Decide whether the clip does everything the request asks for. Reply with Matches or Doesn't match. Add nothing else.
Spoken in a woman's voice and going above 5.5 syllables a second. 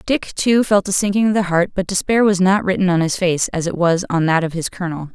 Matches